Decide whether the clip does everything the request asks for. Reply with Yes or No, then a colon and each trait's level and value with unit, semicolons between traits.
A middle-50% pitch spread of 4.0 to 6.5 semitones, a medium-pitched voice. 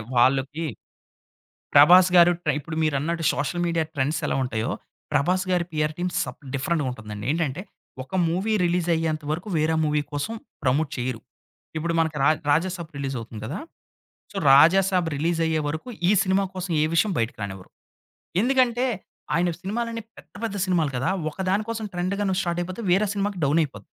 Yes: average, 4.3 semitones; medium, 165 Hz